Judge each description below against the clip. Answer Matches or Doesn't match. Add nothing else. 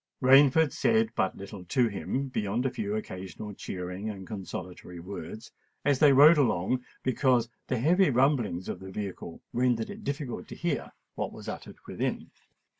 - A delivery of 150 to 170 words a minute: Matches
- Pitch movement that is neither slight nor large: Doesn't match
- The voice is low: Matches